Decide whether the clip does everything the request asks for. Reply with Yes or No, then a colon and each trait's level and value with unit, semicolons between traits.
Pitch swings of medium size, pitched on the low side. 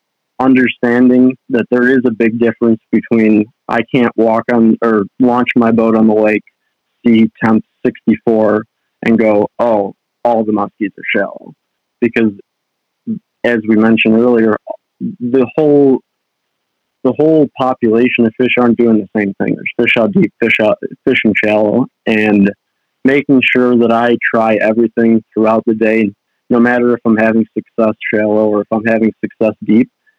No: narrow, 2.0 semitones; low, 115 Hz